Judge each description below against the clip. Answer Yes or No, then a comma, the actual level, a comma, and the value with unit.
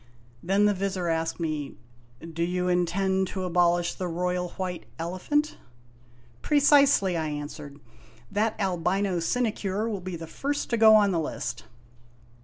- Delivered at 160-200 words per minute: No, average, 150 wpm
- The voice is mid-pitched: Yes, medium, 180 Hz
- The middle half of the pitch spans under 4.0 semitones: Yes, average, 3.4 semitones